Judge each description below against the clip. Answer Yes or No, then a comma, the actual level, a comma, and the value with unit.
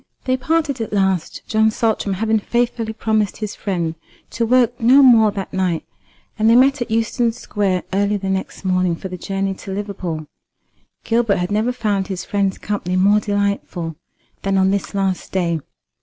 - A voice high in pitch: Yes, high, 205 Hz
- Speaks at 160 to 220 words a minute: Yes, average, 170 wpm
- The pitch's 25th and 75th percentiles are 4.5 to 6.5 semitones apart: No, average, 3.0 semitones